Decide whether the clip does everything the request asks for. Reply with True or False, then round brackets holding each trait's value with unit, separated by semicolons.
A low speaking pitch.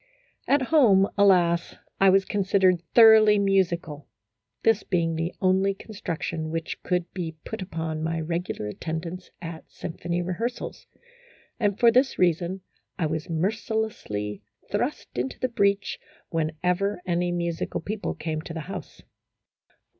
False (180 Hz)